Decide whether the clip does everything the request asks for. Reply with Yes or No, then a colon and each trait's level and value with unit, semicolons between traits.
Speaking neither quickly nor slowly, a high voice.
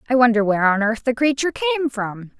No: fast, 225 wpm; high, 245 Hz